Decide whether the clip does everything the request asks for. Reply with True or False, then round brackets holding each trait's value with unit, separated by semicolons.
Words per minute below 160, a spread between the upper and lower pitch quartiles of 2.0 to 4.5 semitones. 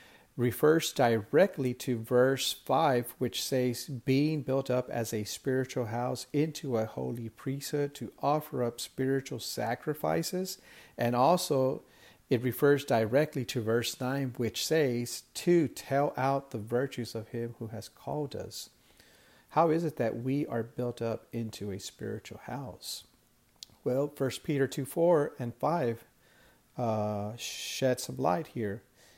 True (140 wpm; 3.2 semitones)